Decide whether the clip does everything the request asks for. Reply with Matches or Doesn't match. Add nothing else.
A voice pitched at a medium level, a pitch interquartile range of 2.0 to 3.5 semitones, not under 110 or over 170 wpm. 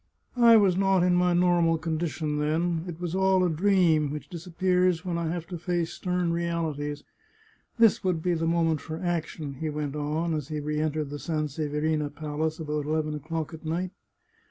Doesn't match